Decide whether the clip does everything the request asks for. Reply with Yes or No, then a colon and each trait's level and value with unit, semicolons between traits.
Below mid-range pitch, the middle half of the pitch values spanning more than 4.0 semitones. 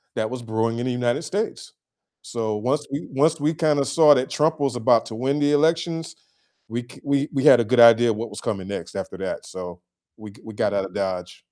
Yes: low, 125 Hz; average, 4.9 semitones